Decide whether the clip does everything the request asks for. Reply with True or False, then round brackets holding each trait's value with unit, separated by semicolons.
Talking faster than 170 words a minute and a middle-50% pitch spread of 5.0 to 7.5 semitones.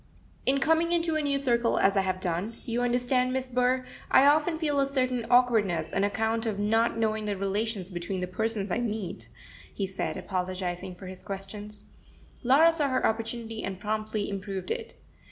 False (180 wpm; 4.6 semitones)